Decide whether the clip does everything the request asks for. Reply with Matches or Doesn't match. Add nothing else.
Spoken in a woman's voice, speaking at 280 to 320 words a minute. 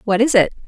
Doesn't match